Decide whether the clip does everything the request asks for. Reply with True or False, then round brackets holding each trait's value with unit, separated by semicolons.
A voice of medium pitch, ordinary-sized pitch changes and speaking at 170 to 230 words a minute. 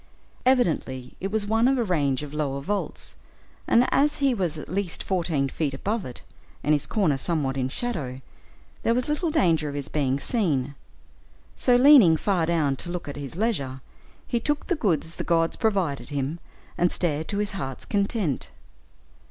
False (170 Hz; 7.5 semitones; 175 wpm)